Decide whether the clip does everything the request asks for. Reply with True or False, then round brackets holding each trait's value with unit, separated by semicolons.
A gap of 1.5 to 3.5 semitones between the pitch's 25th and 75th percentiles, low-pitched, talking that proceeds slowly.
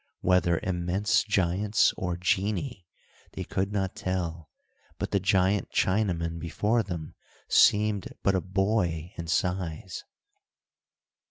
True (2.9 semitones; 95 Hz; 110 wpm)